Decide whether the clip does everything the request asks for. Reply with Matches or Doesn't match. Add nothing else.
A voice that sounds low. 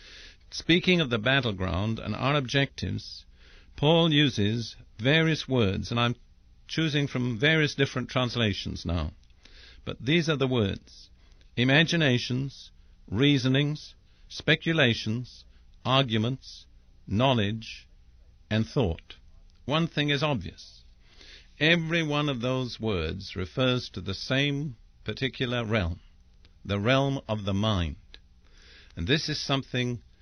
Matches